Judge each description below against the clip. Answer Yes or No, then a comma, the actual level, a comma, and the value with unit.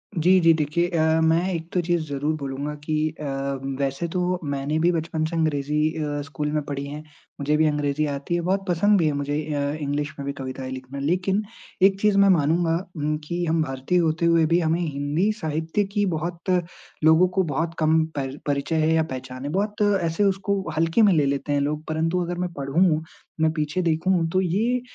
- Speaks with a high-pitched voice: No, medium, 160 Hz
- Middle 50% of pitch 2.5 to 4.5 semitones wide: Yes, average, 3.3 semitones